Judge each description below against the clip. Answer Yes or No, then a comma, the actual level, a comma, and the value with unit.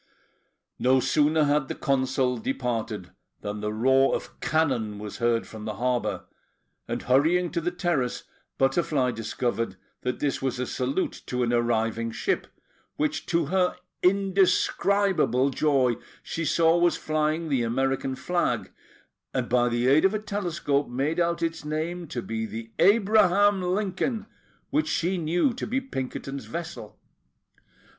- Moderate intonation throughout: No, wide, 6.1 semitones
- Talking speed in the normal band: Yes, average, 145 wpm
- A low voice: No, medium, 145 Hz